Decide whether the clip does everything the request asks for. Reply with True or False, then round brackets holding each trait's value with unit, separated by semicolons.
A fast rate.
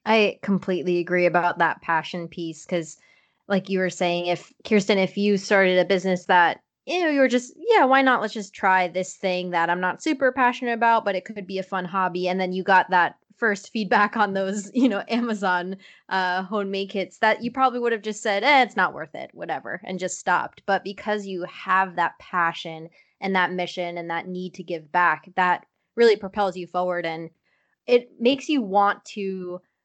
True (210 wpm)